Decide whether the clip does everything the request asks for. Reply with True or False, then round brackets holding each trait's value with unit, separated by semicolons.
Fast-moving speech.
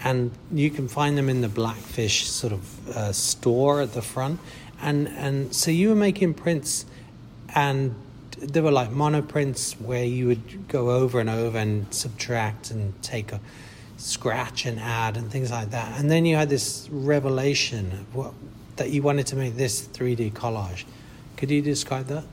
False (175 wpm)